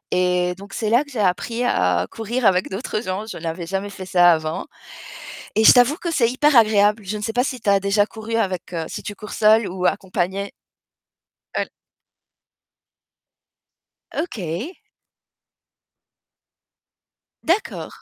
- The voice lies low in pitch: No, high, 205 Hz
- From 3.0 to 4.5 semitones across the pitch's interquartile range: Yes, average, 3.9 semitones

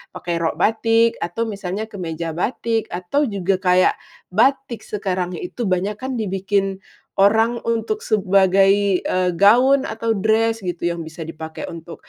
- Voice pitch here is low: No, high, 200 Hz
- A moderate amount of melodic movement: Yes, average, 3.8 semitones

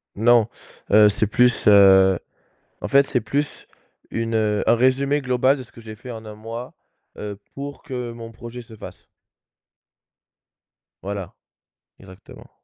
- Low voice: Yes, low, 115 Hz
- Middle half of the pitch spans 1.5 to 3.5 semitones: Yes, average, 3.2 semitones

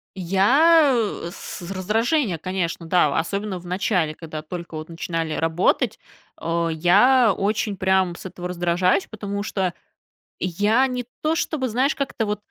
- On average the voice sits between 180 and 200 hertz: Yes, high, 190 Hz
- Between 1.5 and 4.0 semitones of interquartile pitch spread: No, average, 4.5 semitones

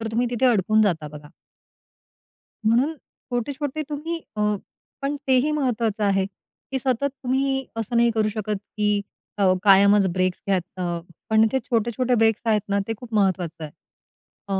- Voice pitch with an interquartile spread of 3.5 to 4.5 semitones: Yes, average, 4.1 semitones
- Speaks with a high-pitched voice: Yes, high, 220 Hz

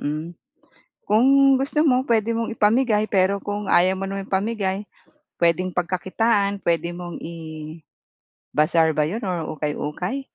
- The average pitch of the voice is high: Yes, high, 195 Hz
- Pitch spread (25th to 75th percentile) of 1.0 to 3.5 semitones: No, average, 4.8 semitones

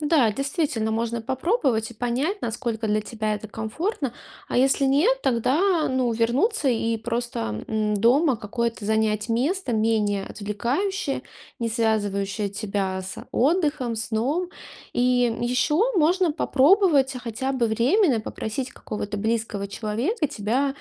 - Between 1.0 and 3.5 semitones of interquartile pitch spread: No, average, 4.3 semitones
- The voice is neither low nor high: No, high, 235 Hz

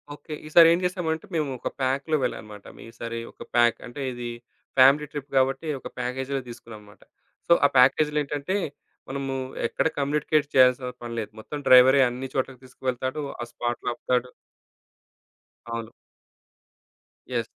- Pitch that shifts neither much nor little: Yes, average, 3.1 semitones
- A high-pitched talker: No, low, 130 Hz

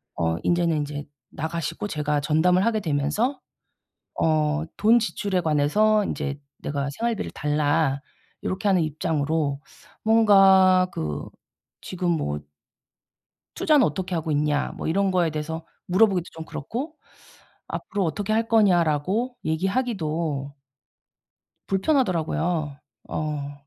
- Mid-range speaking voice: Yes, medium, 165 Hz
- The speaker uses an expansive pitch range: No, average, 4.9 semitones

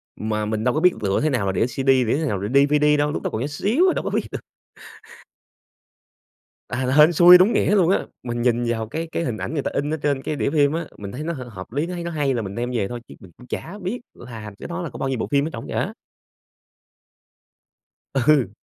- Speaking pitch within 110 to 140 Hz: Yes, low, 135 Hz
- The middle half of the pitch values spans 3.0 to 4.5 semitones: No, wide, 5.5 semitones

